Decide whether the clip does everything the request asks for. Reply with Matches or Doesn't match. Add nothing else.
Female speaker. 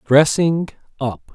Doesn't match